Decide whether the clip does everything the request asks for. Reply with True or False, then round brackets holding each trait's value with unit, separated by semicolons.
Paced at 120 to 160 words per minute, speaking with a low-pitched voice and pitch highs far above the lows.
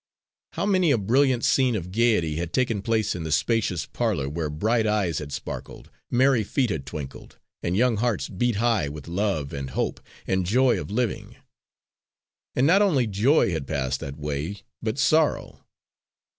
False (170 wpm; 105 Hz; 7.5 semitones)